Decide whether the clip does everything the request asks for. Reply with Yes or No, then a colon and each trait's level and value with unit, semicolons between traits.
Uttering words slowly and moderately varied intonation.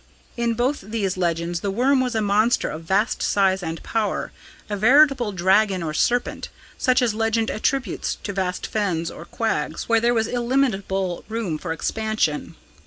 No: average, 165 wpm; average, 4.1 semitones